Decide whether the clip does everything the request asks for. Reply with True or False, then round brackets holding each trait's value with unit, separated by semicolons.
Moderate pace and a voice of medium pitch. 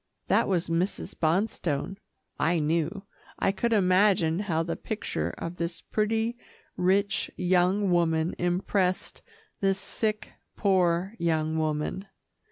False (115 wpm; 180 Hz)